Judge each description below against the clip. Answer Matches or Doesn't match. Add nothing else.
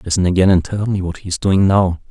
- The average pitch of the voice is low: Matches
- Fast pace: Matches